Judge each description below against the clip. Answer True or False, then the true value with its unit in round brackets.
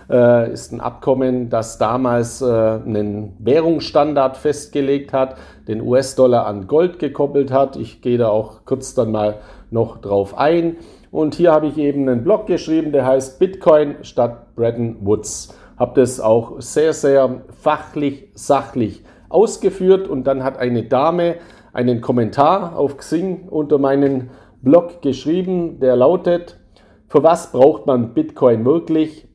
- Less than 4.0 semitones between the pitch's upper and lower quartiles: False (4.5 semitones)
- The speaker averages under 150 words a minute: True (140 wpm)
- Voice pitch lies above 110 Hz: True (135 Hz)